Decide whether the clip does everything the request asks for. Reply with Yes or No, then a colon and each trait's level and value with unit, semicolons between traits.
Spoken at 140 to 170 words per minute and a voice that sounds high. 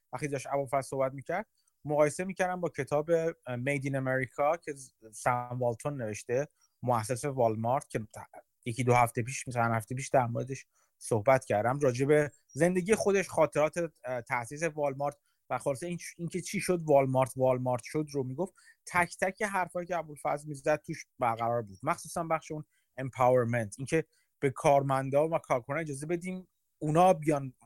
No: fast, 155 wpm; medium, 140 Hz